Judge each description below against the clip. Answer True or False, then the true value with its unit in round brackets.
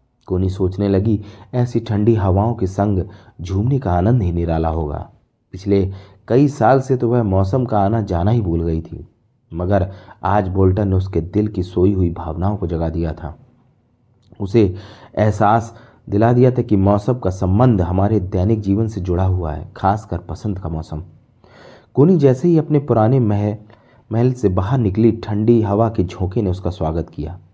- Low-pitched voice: True (100 Hz)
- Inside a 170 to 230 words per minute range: True (175 wpm)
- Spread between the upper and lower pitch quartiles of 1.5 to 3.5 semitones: False (4.1 semitones)